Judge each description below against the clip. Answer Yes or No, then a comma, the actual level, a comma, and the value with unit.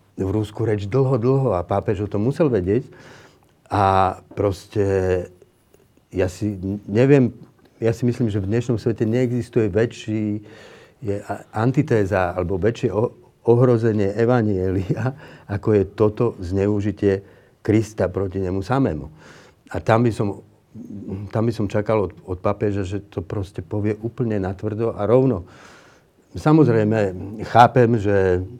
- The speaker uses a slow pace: No, average, 130 wpm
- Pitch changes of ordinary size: Yes, average, 3.0 semitones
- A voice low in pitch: Yes, low, 105 Hz